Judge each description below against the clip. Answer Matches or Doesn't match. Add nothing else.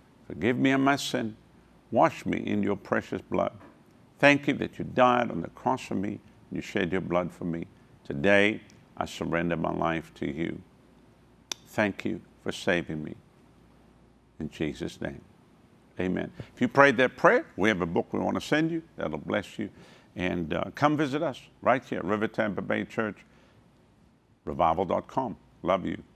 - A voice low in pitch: Matches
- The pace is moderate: Matches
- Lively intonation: Matches